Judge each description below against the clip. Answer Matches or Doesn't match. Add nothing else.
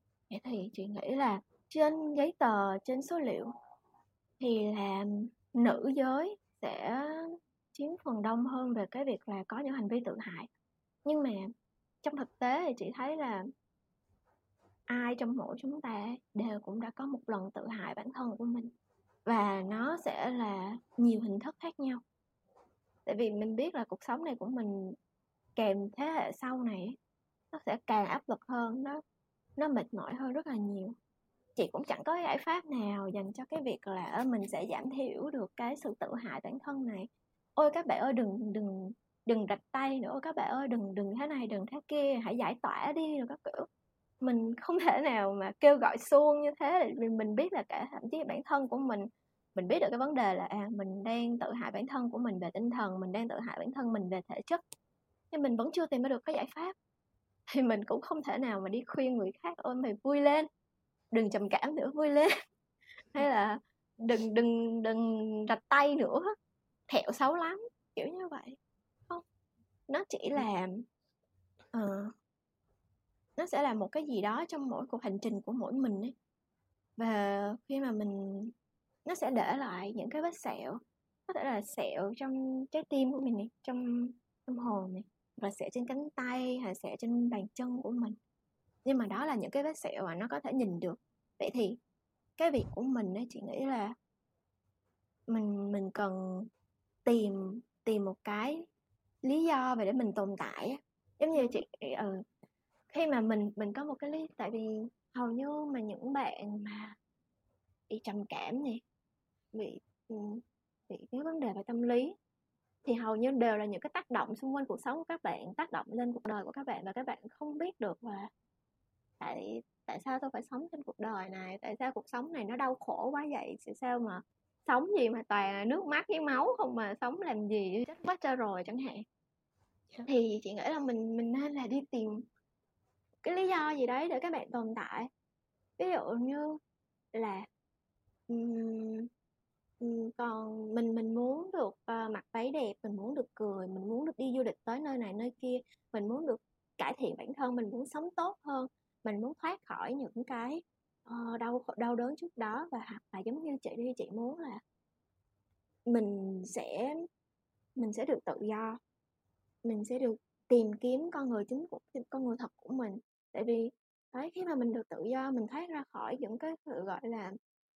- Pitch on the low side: Doesn't match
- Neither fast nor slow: Matches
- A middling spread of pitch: Matches